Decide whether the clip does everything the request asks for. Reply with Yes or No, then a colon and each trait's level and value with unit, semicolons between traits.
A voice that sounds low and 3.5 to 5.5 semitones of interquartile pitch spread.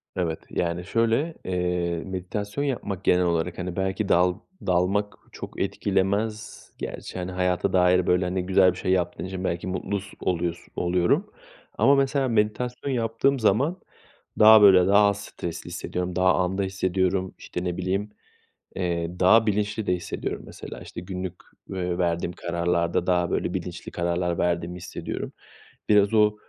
No: very low, 95 Hz; narrow, 2.6 semitones